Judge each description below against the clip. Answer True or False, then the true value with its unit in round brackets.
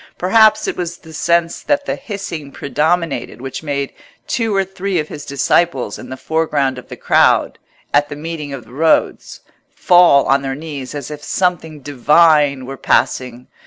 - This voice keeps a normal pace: True (170 wpm)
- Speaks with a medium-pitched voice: True (150 Hz)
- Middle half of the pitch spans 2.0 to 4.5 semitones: True (3.9 semitones)